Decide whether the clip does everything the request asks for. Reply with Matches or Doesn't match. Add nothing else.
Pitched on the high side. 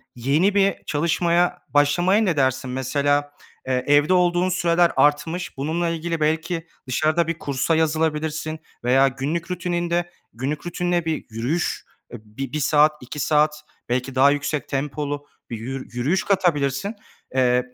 Doesn't match